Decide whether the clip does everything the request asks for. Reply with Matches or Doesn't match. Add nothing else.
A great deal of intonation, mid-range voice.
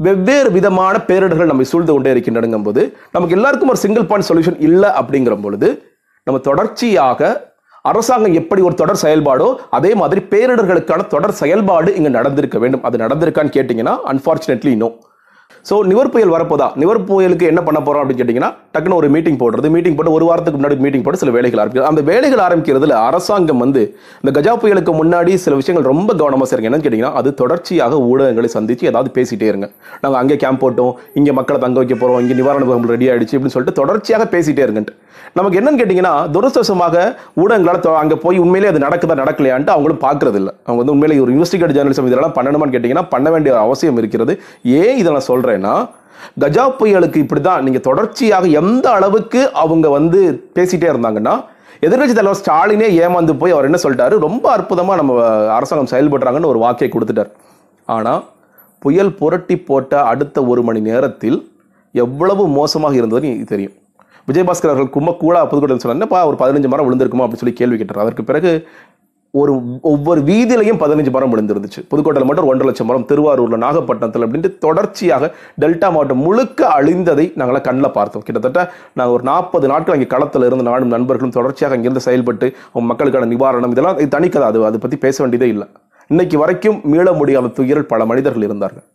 Matches